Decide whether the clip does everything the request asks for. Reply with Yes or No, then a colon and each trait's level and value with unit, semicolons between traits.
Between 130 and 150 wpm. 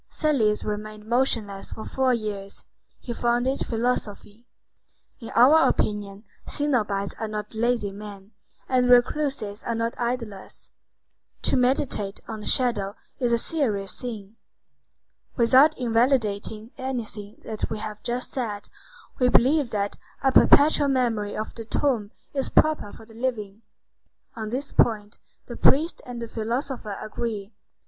Yes: slow, 135 wpm